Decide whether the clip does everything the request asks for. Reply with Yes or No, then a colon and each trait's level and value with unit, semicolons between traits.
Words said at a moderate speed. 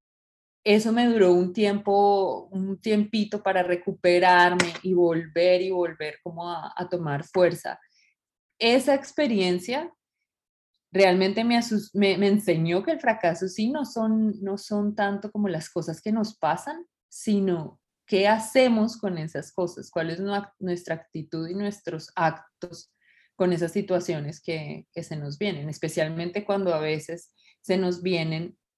Yes: average, 145 wpm